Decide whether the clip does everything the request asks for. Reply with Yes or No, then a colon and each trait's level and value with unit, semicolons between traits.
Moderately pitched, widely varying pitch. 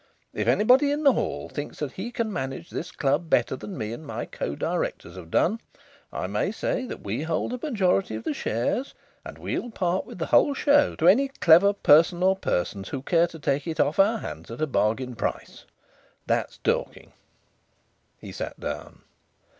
Yes: medium, 170 Hz; wide, 8.4 semitones